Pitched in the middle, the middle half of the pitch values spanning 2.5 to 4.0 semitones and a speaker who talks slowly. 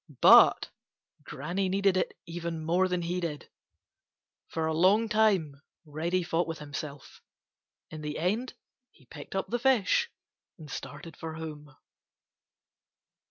Yes: medium, 170 Hz; average, 3.5 semitones; slow, 130 wpm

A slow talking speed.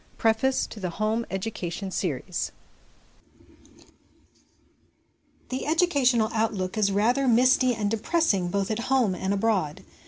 Yes: slow, 120 wpm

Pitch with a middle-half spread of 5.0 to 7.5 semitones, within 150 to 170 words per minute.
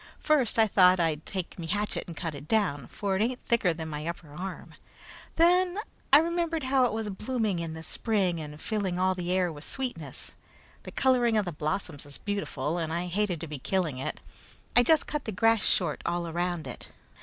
No: wide, 5.5 semitones; fast, 205 wpm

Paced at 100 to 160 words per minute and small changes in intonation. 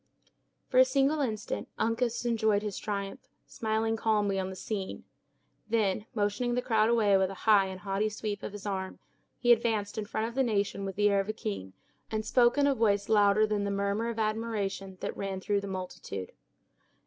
No: average, 195 wpm; narrow, 2.3 semitones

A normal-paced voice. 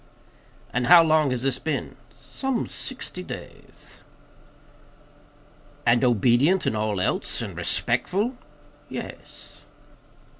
No: slow, 100 wpm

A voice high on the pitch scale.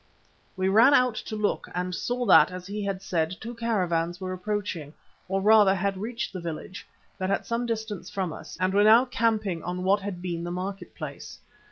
Yes: high, 195 Hz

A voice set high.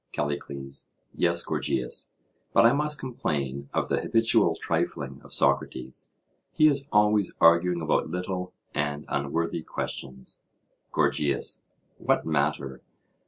No: very low, 80 Hz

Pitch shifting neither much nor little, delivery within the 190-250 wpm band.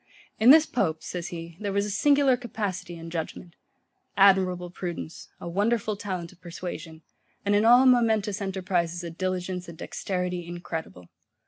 No: average, 3.2 semitones; average, 150 wpm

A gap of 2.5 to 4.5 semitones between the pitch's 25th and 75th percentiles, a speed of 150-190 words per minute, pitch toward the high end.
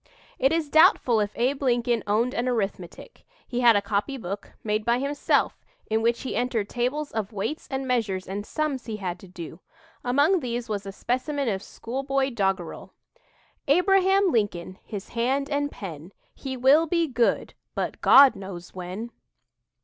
No: average, 5.2 semitones; average, 160 wpm; high, 240 Hz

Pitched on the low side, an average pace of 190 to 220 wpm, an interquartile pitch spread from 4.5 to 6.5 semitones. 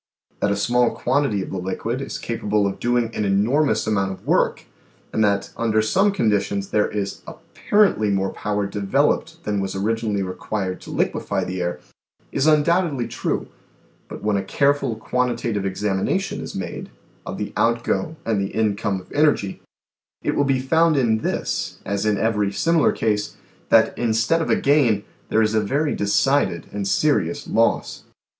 No: low, 110 Hz; average, 165 wpm; average, 4.8 semitones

